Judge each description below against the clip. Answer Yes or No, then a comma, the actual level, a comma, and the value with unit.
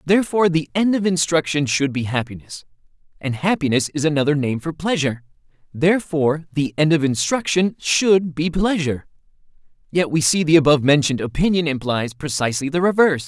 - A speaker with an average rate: Yes, average, 150 wpm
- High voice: No, medium, 155 Hz